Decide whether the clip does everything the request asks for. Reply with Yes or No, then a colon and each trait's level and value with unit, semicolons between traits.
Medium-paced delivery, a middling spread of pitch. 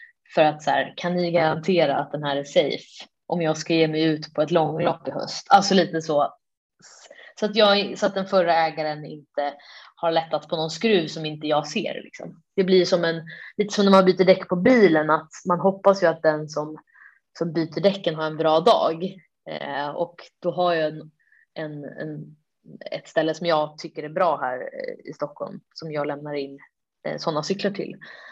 No: fast, 205 wpm; average, 3.4 semitones